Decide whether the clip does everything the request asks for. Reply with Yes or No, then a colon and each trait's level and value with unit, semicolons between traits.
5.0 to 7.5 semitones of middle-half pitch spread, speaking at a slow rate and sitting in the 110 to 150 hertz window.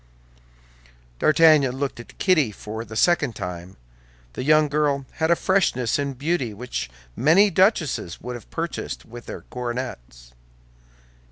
Yes: wide, 5.5 semitones; slow, 125 wpm; low, 135 Hz